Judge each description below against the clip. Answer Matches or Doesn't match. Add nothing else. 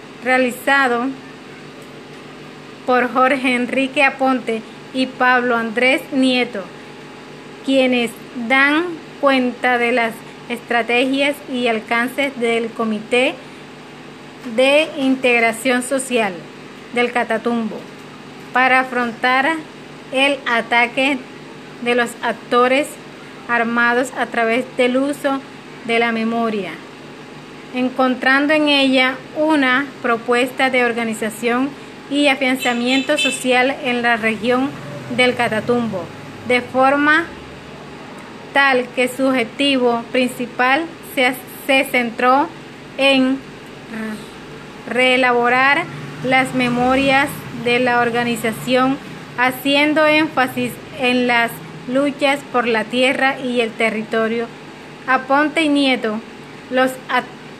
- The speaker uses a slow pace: Matches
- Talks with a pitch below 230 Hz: Doesn't match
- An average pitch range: Doesn't match